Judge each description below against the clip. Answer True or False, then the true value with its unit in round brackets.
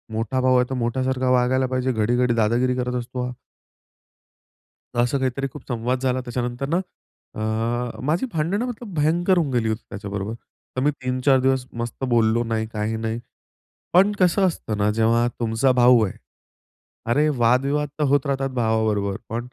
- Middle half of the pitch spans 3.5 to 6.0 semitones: False (2.7 semitones)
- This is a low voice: True (125 Hz)